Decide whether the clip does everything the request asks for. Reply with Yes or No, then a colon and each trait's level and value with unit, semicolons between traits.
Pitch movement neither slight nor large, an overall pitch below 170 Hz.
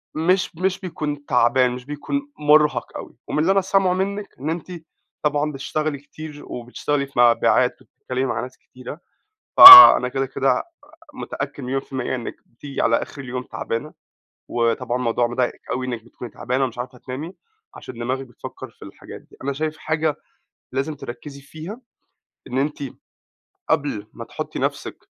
Yes: average, 3.6 semitones; medium, 140 Hz